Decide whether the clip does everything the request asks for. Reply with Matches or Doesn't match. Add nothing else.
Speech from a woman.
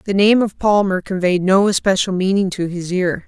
Matches